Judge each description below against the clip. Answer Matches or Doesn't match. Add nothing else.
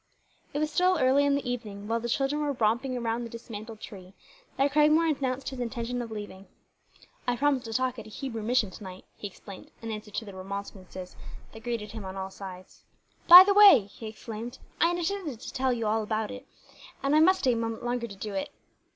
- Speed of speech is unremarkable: Doesn't match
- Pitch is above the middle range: Matches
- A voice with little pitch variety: Doesn't match